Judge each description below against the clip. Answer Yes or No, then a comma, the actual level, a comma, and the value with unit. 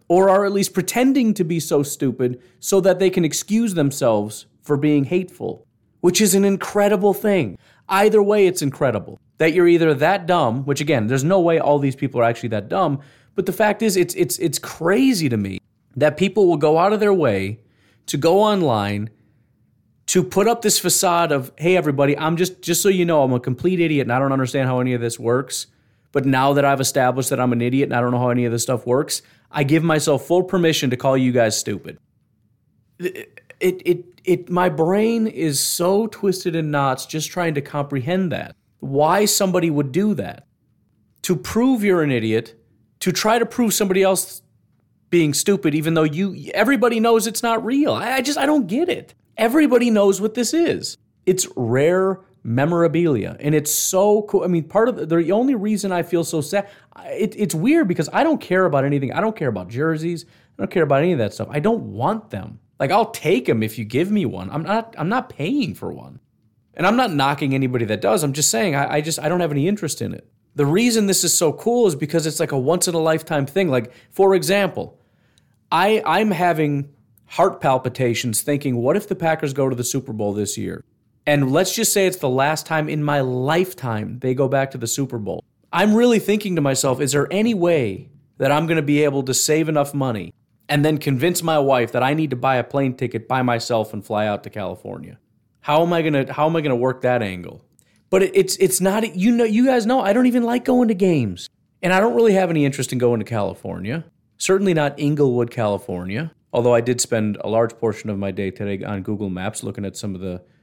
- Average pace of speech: No, fast, 225 wpm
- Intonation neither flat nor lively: No, wide, 7.1 semitones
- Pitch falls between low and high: Yes, medium, 155 Hz